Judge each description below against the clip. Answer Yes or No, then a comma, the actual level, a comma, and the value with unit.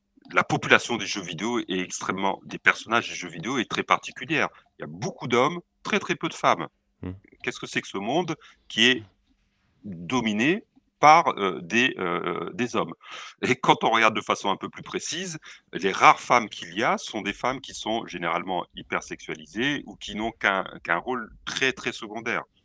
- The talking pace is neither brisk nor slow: Yes, average, 190 wpm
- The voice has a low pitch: Yes, low, 130 Hz